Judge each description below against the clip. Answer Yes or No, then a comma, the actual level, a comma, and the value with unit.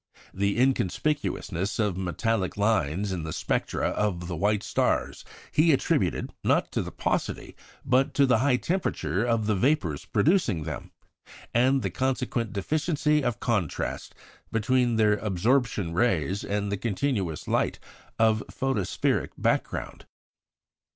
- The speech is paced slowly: Yes, slow, 130 wpm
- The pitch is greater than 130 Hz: No, low, 110 Hz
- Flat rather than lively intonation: No, average, 5.3 semitones